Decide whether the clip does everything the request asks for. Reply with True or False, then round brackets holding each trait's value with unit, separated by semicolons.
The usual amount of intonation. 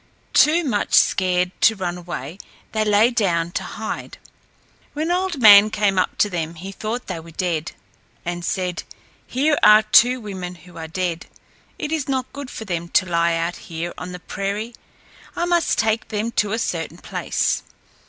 True (4.6 semitones)